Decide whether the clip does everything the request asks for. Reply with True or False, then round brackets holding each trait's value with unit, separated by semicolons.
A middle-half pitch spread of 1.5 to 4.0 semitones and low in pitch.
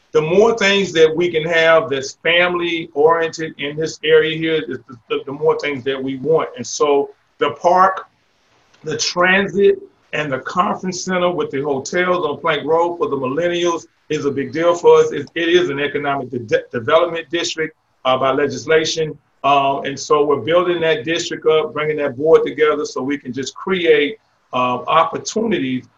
False (3.4 semitones; 160 Hz)